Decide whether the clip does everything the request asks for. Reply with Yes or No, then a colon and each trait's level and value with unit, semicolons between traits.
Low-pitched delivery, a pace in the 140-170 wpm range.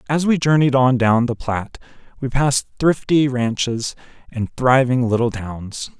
Yes: low, 125 Hz; average, 150 wpm